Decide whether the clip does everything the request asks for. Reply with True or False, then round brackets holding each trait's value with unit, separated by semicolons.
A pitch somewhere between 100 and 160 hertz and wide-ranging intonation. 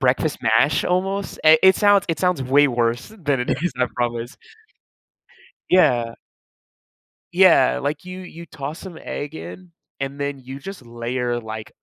True (140 Hz; 6.7 semitones)